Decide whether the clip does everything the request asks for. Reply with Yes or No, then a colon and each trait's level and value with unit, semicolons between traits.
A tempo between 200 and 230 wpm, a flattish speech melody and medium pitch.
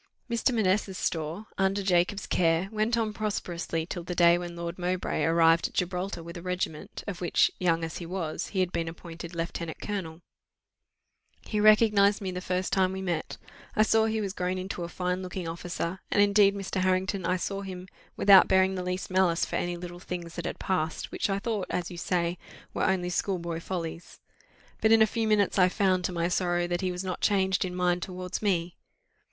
Yes: fast, 205 wpm; narrow, 2.1 semitones; medium, 180 Hz